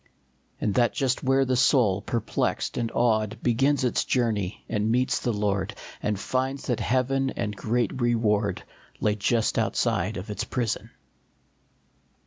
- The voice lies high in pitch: No, low, 115 Hz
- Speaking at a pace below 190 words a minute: Yes, average, 145 wpm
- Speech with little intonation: No, average, 3.4 semitones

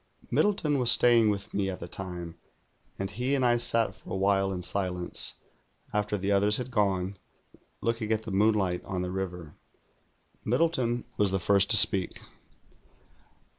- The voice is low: Yes, low, 100 Hz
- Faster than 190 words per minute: No, average, 165 wpm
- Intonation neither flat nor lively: Yes, average, 3.4 semitones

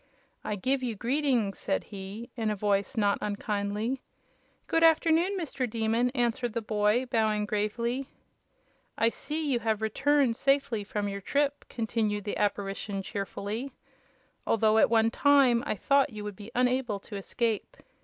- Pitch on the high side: Yes, high, 225 Hz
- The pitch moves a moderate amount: Yes, average, 3.7 semitones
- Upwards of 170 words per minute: No, average, 150 wpm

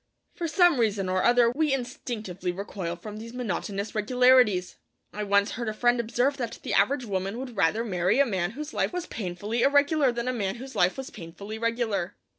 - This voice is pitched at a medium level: No, high, 230 Hz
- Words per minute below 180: No, average, 195 wpm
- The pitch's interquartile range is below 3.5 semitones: No, average, 4.3 semitones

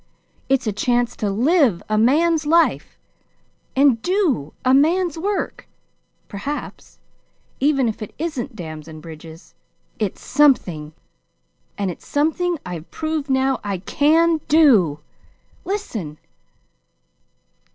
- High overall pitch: Yes, very high, 265 Hz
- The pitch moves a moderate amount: No, wide, 8.1 semitones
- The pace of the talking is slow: Yes, slow, 110 wpm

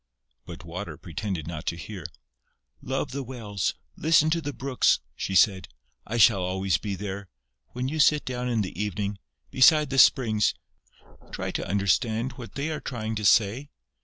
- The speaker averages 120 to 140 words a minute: No, average, 165 wpm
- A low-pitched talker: Yes, low, 110 Hz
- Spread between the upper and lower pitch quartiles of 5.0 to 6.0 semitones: Yes, average, 5.3 semitones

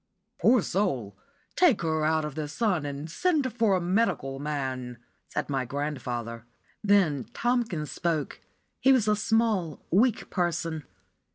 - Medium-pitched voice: Yes, medium, 165 Hz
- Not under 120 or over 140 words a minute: Yes, slow, 135 wpm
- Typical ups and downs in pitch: No, wide, 7.0 semitones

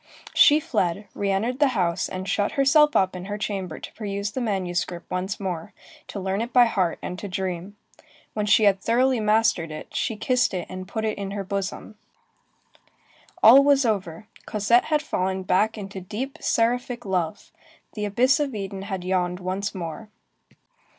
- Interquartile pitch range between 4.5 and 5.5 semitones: No, average, 3.5 semitones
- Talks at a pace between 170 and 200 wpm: Yes, average, 175 wpm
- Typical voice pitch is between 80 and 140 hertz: No, high, 200 Hz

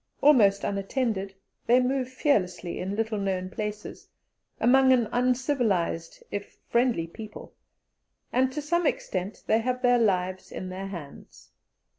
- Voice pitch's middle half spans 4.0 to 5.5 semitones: Yes, average, 5.0 semitones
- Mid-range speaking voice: No, high, 215 Hz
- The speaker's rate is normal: No, slow, 130 wpm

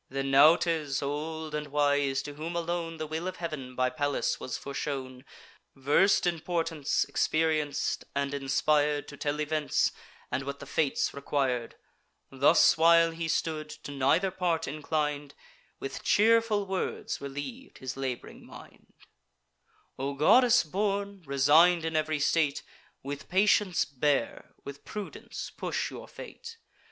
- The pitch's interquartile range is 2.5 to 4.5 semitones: Yes, average, 3.1 semitones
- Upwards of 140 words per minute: No, slow, 135 wpm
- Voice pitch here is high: No, medium, 150 Hz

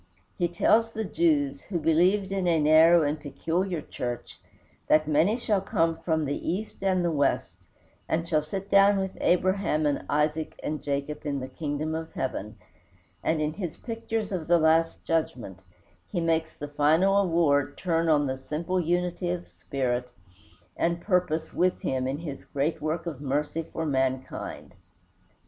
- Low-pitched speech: No, medium, 160 Hz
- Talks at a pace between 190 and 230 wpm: No, average, 165 wpm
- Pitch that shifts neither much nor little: Yes, average, 3.6 semitones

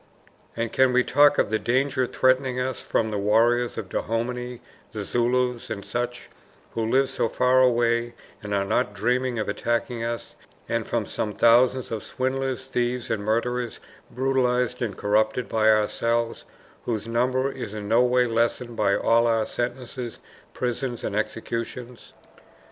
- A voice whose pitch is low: Yes, low, 120 Hz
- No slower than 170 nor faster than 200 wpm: No, average, 155 wpm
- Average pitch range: No, narrow, 2.0 semitones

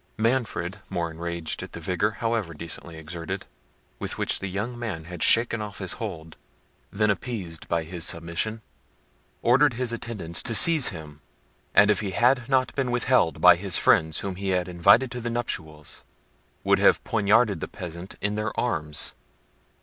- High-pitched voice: No, low, 100 Hz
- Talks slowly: No, average, 165 wpm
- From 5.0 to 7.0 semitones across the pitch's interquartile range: Yes, wide, 5.6 semitones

